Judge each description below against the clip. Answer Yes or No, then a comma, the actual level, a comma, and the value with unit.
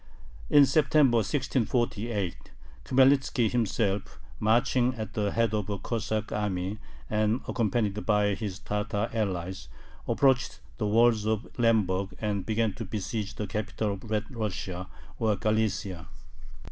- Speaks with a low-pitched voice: Yes, low, 110 Hz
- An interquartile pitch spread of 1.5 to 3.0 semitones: Yes, narrow, 2.4 semitones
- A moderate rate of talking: No, slow, 125 wpm